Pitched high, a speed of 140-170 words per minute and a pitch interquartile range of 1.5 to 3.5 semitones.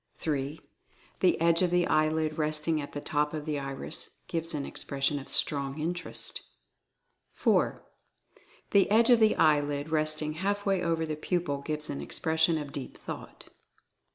No: medium, 155 Hz; average, 155 wpm; narrow, 2.4 semitones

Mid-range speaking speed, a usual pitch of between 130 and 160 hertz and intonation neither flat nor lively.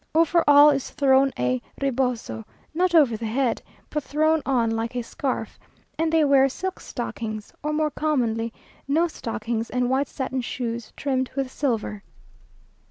No: average, 155 wpm; very high, 265 Hz; average, 4.3 semitones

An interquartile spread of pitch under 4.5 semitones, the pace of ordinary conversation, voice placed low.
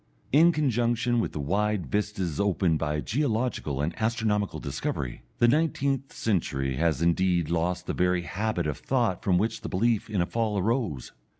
No: wide, 5.5 semitones; average, 165 wpm; low, 100 Hz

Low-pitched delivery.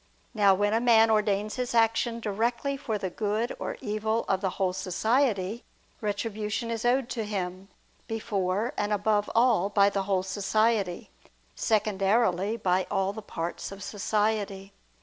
No: high, 210 Hz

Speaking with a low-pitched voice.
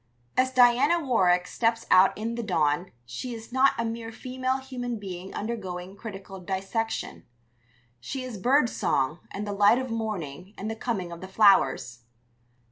No: high, 220 Hz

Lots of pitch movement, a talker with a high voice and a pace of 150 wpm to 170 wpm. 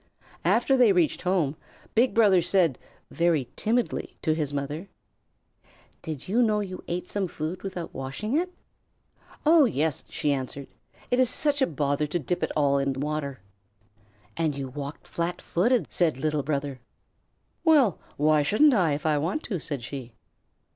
No: wide, 6.3 semitones; medium, 160 Hz; average, 160 wpm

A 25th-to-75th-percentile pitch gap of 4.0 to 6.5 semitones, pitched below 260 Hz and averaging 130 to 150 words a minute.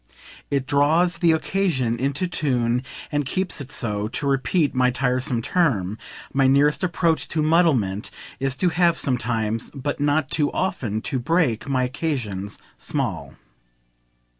Yes: average, 4.7 semitones; medium, 140 Hz; average, 140 wpm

